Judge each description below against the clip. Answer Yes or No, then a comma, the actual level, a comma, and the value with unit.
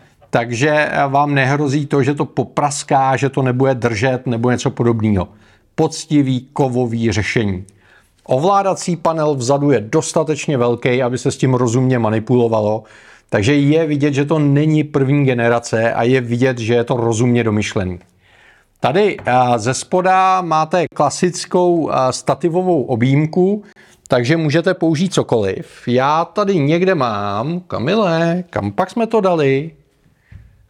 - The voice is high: No, medium, 140 Hz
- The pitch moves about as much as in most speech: Yes, average, 4.9 semitones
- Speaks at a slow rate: No, average, 130 wpm